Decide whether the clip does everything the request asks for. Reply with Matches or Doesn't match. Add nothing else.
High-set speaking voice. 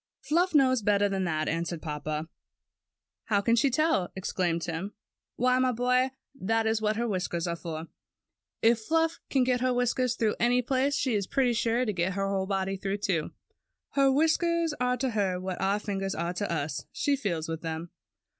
Matches